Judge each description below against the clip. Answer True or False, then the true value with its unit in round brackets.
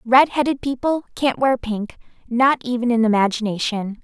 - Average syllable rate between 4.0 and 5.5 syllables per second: True (4.9 syllables/s)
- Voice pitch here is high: True (240 Hz)